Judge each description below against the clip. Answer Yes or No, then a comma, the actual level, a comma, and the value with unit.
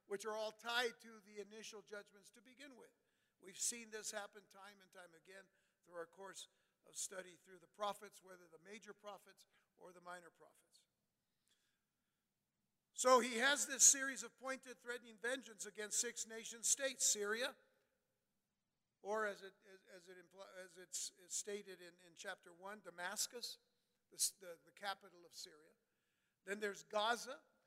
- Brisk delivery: No, average, 155 wpm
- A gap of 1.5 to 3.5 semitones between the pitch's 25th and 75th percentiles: No, average, 3.9 semitones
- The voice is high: Yes, high, 205 Hz